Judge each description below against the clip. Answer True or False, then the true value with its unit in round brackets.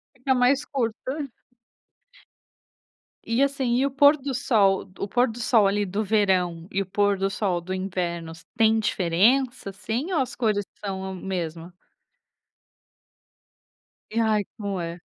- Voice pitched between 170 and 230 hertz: True (205 Hz)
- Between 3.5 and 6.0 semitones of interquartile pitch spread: True (4.7 semitones)